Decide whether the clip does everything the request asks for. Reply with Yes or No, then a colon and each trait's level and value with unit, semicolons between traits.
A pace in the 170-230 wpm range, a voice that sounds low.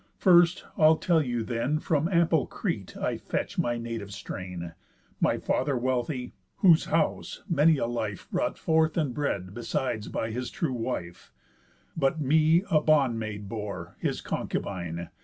No: average, 150 wpm; low, 125 Hz